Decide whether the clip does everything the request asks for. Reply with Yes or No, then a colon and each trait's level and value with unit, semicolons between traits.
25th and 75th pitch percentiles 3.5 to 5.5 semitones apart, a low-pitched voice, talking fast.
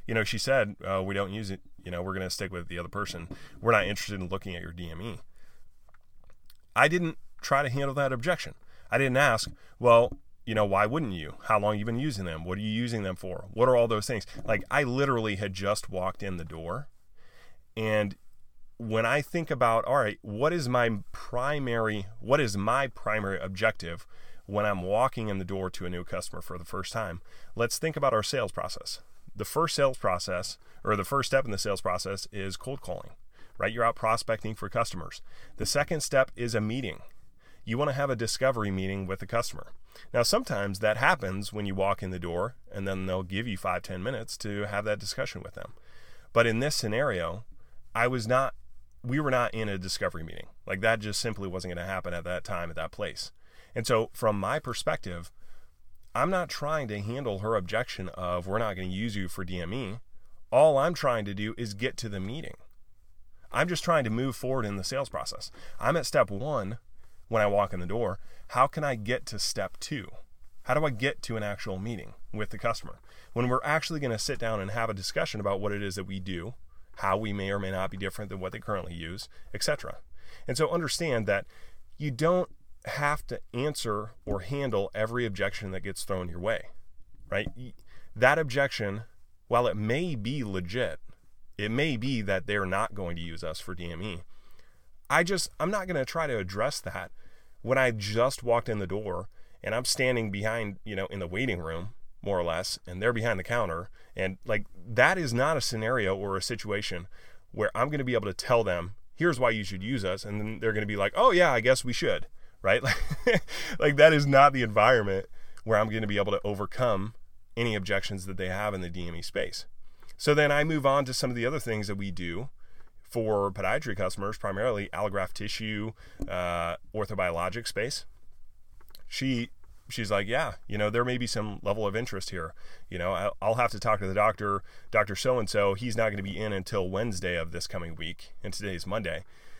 Yes: average, 4.2 semitones; low, 105 Hz; fast, 215 wpm